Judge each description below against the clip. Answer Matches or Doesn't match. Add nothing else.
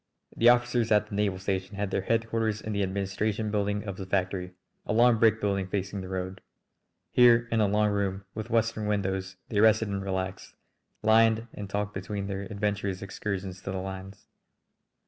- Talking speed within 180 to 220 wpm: Matches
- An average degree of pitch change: Doesn't match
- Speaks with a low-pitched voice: Matches